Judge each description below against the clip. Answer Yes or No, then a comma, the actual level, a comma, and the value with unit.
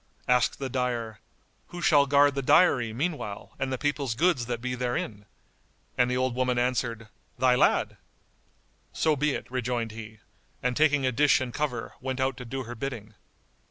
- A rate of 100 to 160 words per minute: No, average, 175 wpm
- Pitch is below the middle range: Yes, low, 125 Hz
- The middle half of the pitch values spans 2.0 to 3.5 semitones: Yes, narrow, 2.6 semitones